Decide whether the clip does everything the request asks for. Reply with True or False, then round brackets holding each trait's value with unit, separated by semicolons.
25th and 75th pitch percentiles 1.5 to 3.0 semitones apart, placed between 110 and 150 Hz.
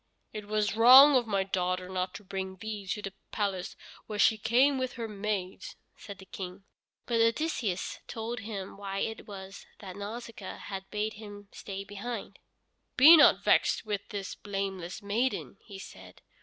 False (2.7 semitones; 205 Hz)